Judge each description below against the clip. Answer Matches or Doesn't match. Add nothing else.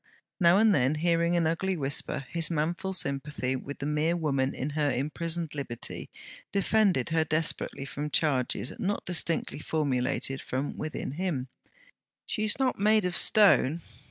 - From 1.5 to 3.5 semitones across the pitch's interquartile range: Doesn't match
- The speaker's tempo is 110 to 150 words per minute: Matches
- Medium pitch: Matches